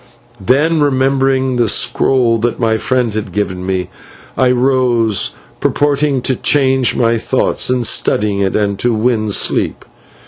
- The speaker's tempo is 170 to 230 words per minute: No, average, 140 wpm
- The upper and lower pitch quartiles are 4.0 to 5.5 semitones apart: No, average, 3.5 semitones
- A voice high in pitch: No, low, 120 Hz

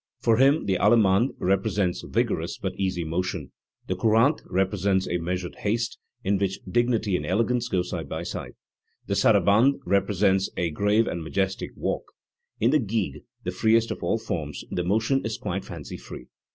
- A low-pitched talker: Yes, low, 100 Hz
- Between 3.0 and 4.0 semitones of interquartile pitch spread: Yes, average, 3.7 semitones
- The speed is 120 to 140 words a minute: No, average, 170 wpm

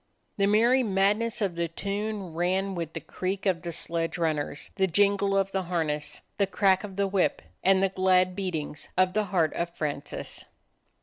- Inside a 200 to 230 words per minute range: No, average, 180 wpm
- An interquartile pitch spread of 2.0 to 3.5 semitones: Yes, average, 2.7 semitones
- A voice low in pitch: No, high, 190 Hz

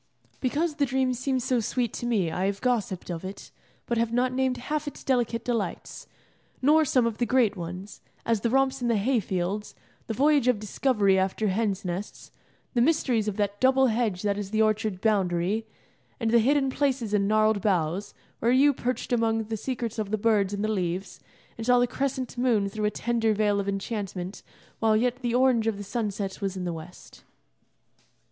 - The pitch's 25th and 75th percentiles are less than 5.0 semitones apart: Yes, average, 3.9 semitones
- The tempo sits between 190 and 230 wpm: Yes, average, 195 wpm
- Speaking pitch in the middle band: No, high, 225 Hz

